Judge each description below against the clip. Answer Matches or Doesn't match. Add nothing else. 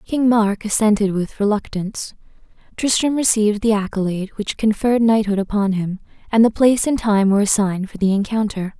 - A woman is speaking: Matches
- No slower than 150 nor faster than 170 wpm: Matches